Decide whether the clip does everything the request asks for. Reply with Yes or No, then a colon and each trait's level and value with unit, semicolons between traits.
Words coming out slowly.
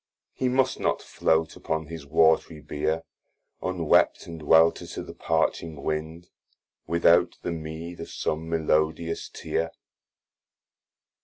Yes: slow, 120 wpm